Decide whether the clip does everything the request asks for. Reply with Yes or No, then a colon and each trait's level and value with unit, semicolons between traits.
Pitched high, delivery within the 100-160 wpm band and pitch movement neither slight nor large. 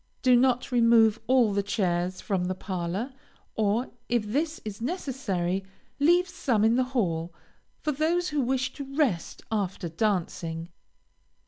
No: high, 225 Hz; average, 140 wpm; wide, 6.1 semitones